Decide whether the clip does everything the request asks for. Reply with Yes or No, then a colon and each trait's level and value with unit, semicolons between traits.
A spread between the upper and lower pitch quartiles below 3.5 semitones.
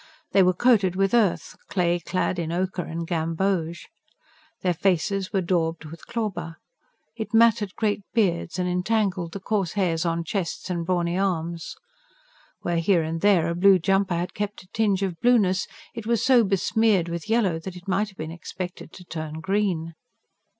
Yes: average, 3.0 semitones